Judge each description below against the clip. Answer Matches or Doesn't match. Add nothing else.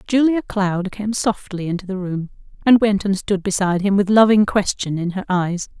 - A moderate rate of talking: Matches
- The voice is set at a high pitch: Matches